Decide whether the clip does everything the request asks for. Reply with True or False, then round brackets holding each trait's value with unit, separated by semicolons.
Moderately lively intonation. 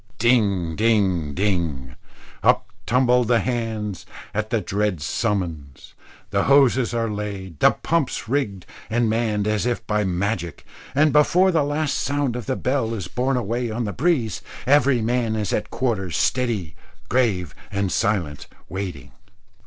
True (4.4 semitones)